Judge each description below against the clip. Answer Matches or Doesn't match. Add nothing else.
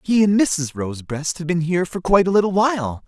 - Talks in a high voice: Doesn't match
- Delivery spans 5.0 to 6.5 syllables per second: Matches